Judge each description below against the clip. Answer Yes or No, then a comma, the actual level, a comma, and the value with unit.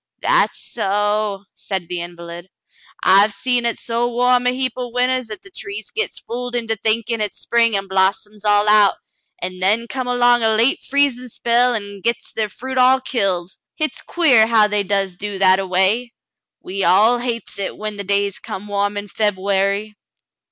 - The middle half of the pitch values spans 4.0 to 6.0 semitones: No, average, 3.5 semitones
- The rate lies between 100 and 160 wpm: No, average, 180 wpm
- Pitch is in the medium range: No, high, 215 Hz